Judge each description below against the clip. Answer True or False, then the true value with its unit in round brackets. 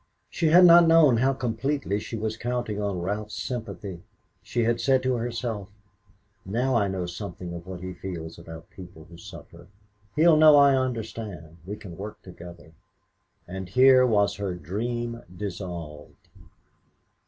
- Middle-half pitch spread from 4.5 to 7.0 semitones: True (5.5 semitones)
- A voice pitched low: True (105 Hz)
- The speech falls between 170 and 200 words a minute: False (150 wpm)